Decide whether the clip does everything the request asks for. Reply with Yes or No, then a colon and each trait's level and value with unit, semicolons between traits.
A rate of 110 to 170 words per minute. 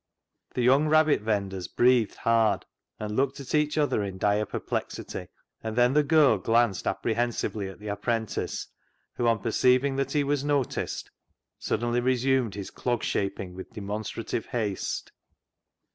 Yes: average, 145 wpm